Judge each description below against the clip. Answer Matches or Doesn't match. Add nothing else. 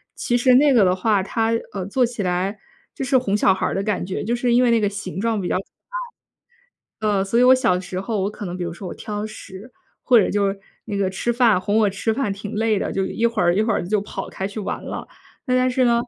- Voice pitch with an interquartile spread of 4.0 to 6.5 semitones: Doesn't match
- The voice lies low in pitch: Doesn't match